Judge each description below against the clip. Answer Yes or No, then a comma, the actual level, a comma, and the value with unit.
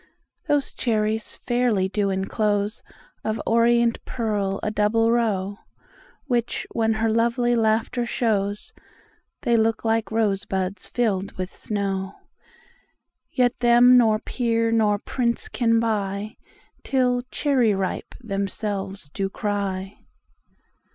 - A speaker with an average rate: No, slow, 95 wpm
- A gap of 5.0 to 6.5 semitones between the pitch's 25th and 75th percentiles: No, average, 2.8 semitones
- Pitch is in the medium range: No, high, 220 Hz